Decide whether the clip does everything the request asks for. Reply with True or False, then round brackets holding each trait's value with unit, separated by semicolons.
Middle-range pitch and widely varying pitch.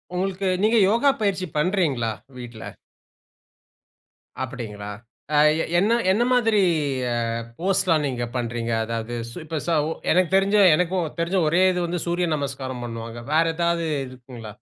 True (165 Hz; 7.6 semitones)